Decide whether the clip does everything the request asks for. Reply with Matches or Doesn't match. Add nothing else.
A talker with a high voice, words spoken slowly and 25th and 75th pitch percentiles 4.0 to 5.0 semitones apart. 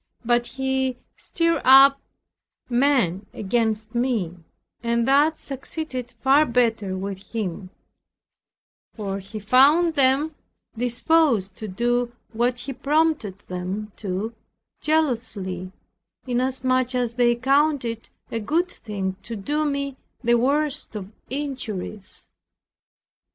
Matches